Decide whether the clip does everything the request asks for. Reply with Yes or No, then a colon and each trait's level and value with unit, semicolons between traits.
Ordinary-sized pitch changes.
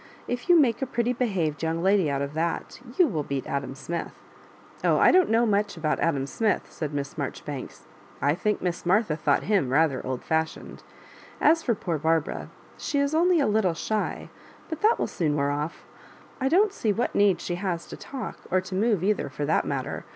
No: wide, 7.4 semitones